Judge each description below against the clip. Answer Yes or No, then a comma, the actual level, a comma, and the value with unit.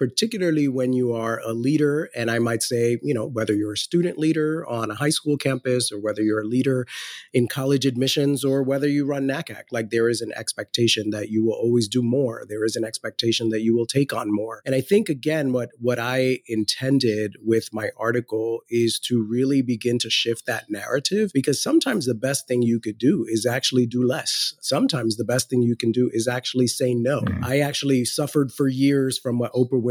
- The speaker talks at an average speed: No, fast, 215 wpm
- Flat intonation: No, average, 3.2 semitones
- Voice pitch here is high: No, low, 125 Hz